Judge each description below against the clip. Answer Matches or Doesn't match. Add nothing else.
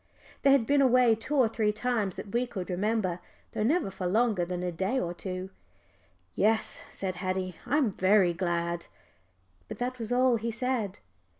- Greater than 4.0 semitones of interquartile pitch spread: Matches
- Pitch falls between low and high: Doesn't match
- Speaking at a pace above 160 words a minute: Matches